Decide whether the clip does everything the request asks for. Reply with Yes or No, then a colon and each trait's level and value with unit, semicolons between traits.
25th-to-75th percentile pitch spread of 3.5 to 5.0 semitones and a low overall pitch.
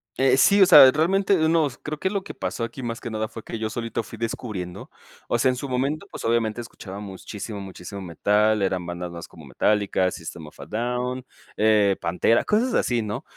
Yes: average, 4.5 semitones; low, 115 Hz